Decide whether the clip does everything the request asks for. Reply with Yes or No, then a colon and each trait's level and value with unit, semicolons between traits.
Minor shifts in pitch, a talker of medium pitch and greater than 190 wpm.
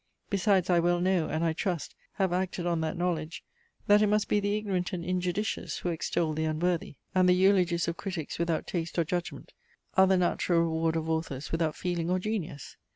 Yes: narrow, 2.3 semitones; medium, 175 Hz; average, 200 wpm